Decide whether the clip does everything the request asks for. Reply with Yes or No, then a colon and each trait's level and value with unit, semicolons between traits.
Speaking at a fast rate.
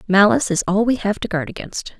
Yes: fast, 240 wpm